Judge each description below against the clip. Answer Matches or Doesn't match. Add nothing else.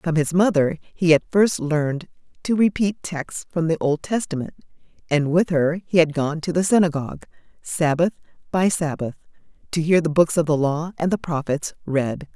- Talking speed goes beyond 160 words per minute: Matches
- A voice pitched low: Doesn't match